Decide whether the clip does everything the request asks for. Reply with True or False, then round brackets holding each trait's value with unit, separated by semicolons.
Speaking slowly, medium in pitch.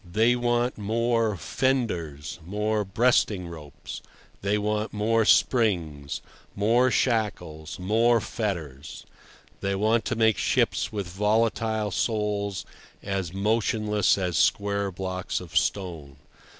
False (110 wpm; 105 Hz)